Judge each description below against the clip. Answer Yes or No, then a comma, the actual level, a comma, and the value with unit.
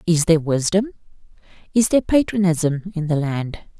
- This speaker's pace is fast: No, average, 140 wpm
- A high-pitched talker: No, medium, 175 Hz